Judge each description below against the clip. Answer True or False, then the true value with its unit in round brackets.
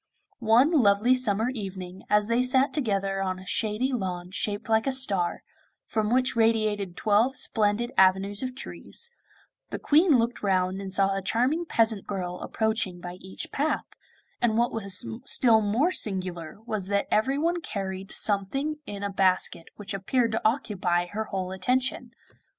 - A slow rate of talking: False (155 wpm)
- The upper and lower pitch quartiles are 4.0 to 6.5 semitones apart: True (4.4 semitones)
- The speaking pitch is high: True (210 Hz)